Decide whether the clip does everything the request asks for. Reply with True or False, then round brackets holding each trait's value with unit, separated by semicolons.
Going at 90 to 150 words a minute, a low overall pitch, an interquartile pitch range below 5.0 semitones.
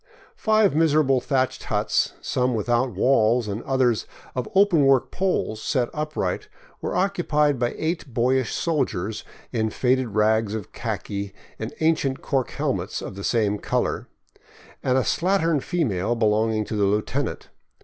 False (145 wpm; 125 Hz; 5.5 semitones)